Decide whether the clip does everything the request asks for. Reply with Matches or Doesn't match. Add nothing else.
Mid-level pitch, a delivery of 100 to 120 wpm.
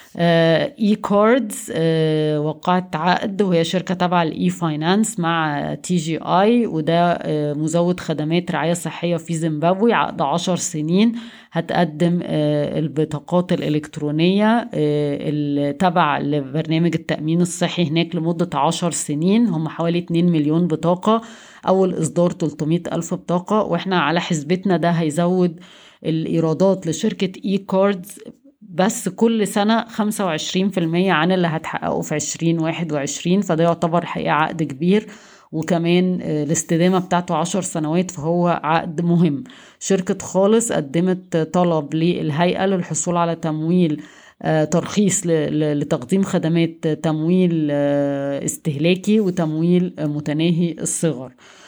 Matches